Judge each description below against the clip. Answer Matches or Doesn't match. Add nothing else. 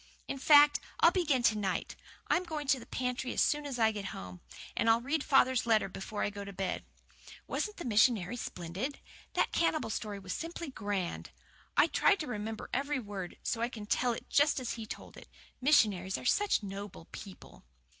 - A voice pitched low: Doesn't match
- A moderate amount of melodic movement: Doesn't match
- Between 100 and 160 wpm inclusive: Doesn't match